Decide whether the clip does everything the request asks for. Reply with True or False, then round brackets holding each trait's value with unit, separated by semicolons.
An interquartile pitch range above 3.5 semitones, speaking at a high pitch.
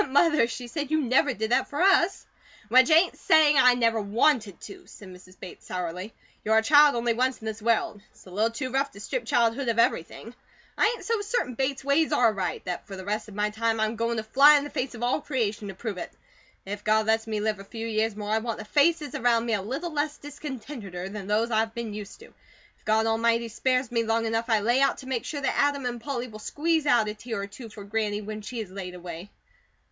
True (4.2 semitones; 230 Hz)